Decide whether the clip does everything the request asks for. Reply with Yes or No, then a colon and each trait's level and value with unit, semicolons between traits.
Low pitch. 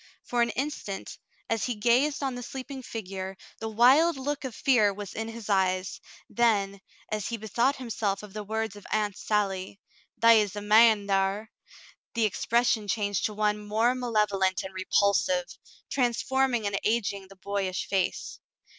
No: high, 215 Hz